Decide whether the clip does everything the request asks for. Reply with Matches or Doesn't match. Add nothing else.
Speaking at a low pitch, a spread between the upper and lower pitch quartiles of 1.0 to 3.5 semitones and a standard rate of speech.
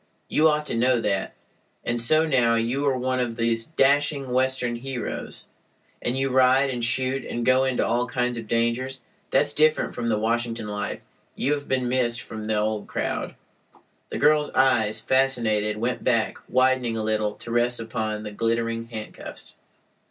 Matches